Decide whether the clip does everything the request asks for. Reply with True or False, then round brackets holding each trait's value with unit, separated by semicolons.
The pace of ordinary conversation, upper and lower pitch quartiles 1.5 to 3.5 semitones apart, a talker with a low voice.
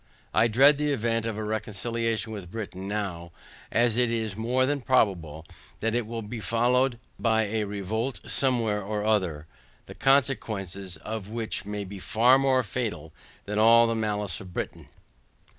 True (160 wpm; 2.8 semitones; 110 Hz)